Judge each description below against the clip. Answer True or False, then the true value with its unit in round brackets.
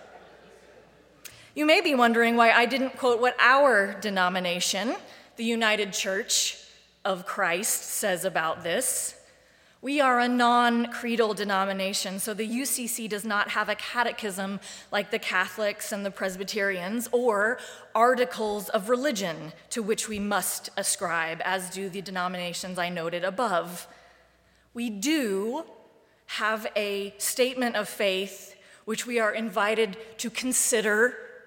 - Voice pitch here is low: False (215 Hz)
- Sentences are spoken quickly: False (130 wpm)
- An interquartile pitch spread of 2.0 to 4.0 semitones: True (3.5 semitones)